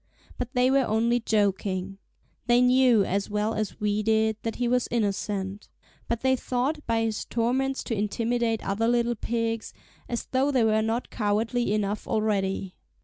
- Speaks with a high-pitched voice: Yes, high, 225 Hz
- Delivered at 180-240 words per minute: No, average, 160 wpm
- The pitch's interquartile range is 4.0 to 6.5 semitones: No, narrow, 2.6 semitones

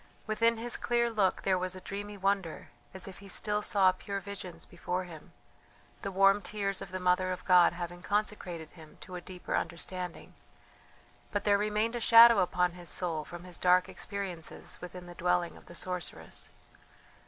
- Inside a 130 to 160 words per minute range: No, average, 175 wpm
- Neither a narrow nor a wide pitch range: No, narrow, 2.3 semitones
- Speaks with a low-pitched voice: No, medium, 185 Hz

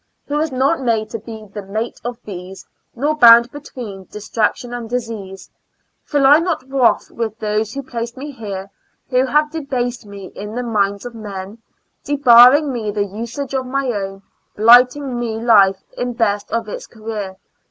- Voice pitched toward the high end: Yes, high, 230 Hz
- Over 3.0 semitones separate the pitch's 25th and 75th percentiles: Yes, average, 3.6 semitones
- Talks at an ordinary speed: Yes, average, 170 wpm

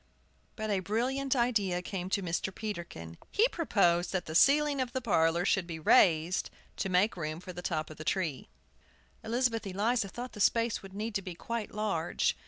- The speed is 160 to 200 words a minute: Yes, average, 190 wpm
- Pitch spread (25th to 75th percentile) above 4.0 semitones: Yes, average, 5.0 semitones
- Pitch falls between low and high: No, high, 195 Hz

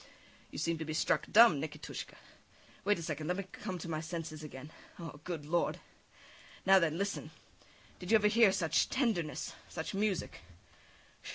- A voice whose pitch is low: No, medium, 170 Hz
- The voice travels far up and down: No, average, 4.1 semitones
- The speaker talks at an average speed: Yes, average, 165 wpm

